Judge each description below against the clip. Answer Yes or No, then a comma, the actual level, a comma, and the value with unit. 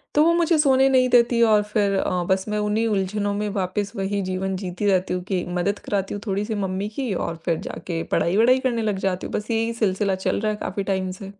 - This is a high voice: Yes, high, 205 Hz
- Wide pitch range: No, average, 2.8 semitones